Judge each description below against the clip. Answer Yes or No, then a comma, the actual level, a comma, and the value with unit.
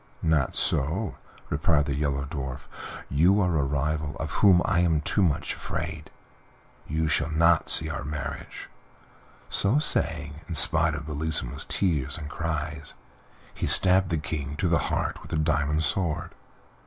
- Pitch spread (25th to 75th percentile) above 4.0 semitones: No, narrow, 2.4 semitones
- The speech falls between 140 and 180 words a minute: Yes, average, 155 wpm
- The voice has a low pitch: Yes, very low, 80 Hz